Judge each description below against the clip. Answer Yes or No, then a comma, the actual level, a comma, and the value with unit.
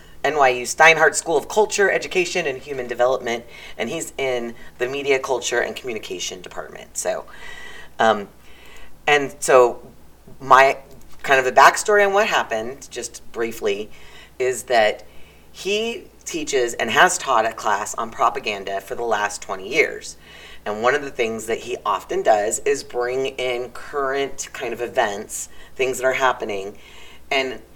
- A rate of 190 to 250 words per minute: No, average, 150 wpm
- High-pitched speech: No, low, 135 Hz